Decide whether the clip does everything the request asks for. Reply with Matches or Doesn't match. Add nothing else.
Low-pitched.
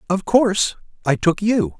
Doesn't match